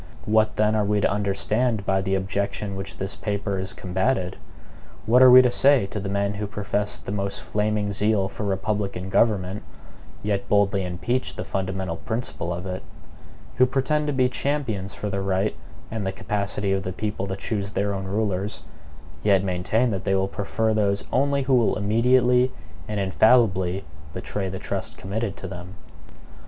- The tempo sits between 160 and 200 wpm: Yes, average, 175 wpm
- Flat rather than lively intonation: Yes, narrow, 2.3 semitones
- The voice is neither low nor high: No, low, 100 Hz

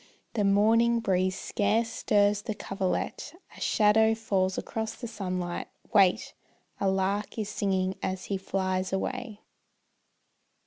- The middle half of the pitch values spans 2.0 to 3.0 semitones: Yes, narrow, 2.6 semitones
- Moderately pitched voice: No, high, 200 Hz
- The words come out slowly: Yes, slow, 125 wpm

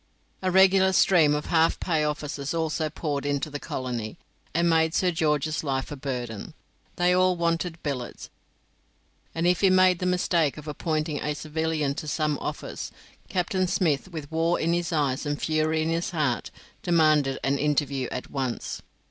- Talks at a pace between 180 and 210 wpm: No, average, 165 wpm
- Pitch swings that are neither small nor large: Yes, average, 3.0 semitones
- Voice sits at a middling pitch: Yes, medium, 155 Hz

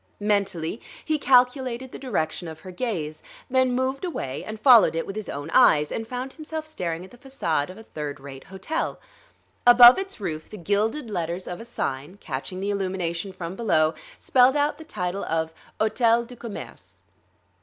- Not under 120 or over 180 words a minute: Yes, average, 175 wpm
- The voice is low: No, high, 205 Hz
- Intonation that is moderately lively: No, wide, 7.0 semitones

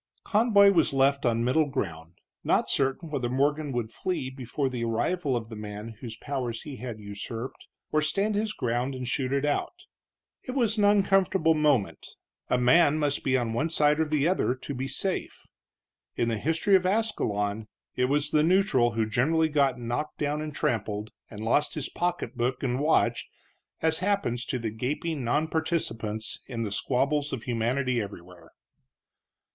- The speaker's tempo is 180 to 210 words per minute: No, average, 170 wpm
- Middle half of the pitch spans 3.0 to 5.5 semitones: Yes, average, 5.1 semitones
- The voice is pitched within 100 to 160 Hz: Yes, low, 135 Hz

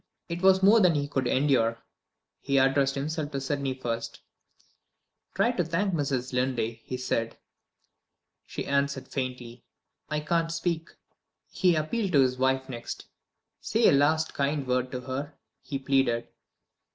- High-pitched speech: No, medium, 140 Hz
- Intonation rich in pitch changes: No, average, 3.7 semitones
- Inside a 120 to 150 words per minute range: Yes, average, 145 wpm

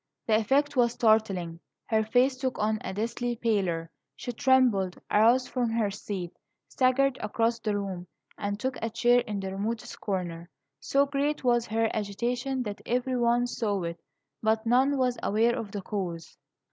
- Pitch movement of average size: Yes, average, 3.4 semitones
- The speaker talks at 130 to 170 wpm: Yes, average, 165 wpm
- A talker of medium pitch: No, high, 225 Hz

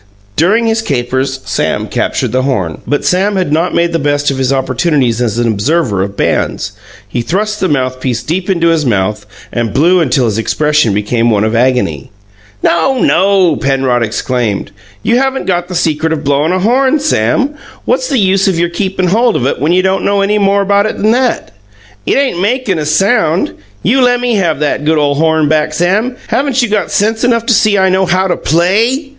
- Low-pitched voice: No, medium, 170 Hz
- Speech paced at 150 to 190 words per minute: No, average, 200 wpm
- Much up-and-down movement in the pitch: Yes, wide, 7.5 semitones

